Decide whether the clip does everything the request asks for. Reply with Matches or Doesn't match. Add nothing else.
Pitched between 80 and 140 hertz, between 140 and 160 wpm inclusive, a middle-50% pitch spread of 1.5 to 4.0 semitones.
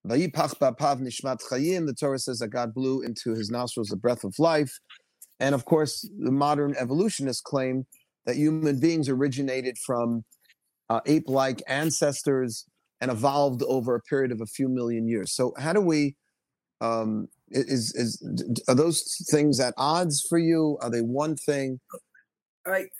Matches